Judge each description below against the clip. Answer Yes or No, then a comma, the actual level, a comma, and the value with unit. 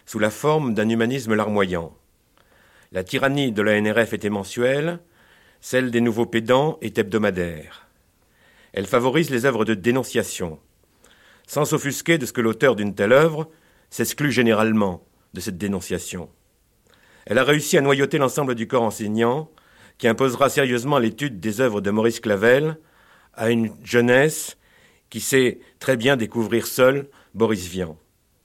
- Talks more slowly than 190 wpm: Yes, slow, 145 wpm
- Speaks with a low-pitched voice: Yes, low, 115 Hz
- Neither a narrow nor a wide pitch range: Yes, average, 4.5 semitones